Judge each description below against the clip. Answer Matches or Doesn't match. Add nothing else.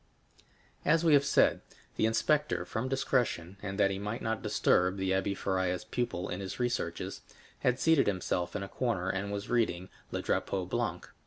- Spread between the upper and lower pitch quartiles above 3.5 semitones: Matches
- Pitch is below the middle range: Matches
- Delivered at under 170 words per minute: Doesn't match